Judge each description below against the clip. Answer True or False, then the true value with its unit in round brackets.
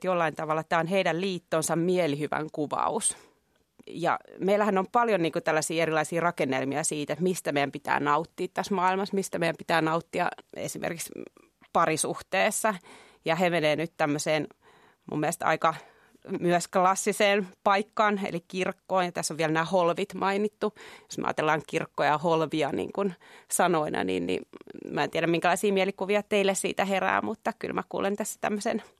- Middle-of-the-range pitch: True (180 Hz)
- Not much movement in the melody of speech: False (3.7 semitones)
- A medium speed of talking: False (160 wpm)